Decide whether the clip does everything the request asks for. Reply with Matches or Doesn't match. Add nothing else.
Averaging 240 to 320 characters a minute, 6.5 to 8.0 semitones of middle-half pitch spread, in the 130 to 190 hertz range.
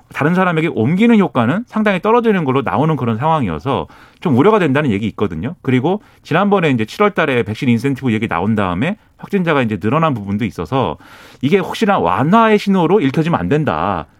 Doesn't match